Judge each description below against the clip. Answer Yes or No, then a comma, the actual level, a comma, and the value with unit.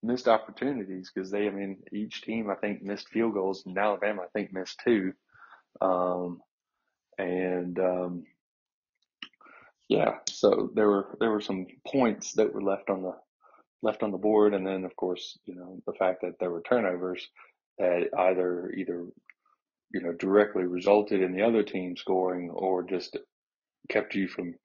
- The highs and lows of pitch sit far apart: No, narrow, 2.4 semitones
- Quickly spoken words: No, average, 165 wpm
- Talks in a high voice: No, very low, 95 Hz